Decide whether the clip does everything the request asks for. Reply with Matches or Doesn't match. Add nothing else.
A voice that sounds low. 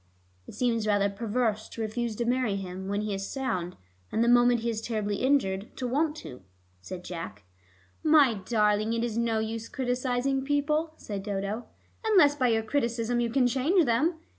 Doesn't match